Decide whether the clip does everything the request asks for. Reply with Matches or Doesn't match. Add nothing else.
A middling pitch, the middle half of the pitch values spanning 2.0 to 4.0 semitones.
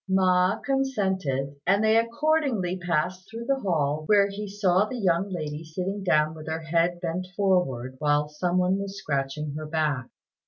Doesn't match